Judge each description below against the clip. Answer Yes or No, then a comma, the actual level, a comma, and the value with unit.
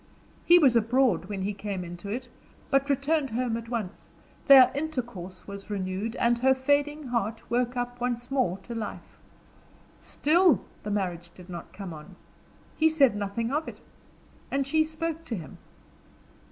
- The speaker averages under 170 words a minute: Yes, average, 160 wpm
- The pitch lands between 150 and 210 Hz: No, high, 240 Hz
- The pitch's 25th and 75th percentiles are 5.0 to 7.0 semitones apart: Yes, wide, 5.5 semitones